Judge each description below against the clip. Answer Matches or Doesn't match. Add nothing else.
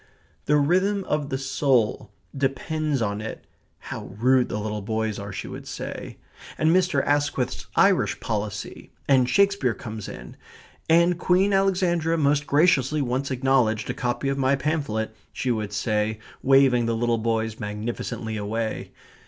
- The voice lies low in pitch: Matches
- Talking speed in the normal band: Matches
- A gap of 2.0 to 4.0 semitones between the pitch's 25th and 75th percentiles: Doesn't match